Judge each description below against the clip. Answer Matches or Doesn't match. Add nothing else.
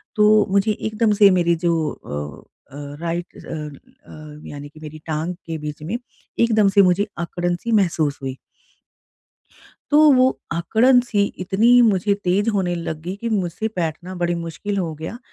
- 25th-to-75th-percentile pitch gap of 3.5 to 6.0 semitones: Matches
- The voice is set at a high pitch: Doesn't match